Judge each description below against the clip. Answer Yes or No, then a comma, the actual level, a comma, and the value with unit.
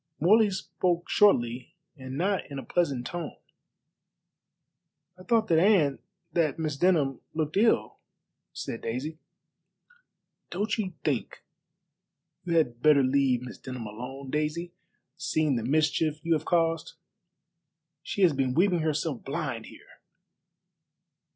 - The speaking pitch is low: No, medium, 155 Hz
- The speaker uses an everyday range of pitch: Yes, average, 4.6 semitones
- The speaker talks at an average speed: No, slow, 125 wpm